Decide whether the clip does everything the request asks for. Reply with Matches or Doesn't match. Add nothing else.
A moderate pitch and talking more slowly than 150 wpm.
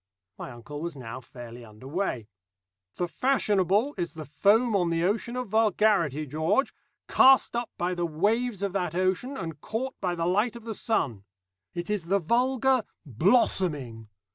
Doesn't match